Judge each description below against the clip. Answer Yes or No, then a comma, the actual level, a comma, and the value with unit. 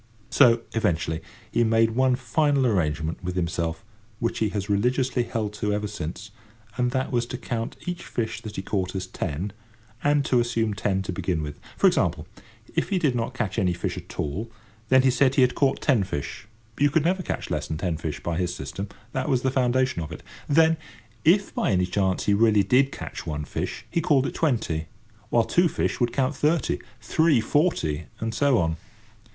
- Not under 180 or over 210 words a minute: Yes, average, 200 wpm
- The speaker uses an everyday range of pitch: No, wide, 6.2 semitones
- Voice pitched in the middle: No, low, 115 Hz